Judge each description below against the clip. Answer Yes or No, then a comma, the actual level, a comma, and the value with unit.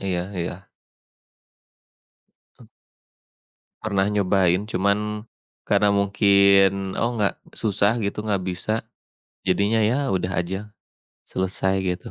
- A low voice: Yes, low, 100 Hz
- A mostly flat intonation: Yes, narrow, 1.8 semitones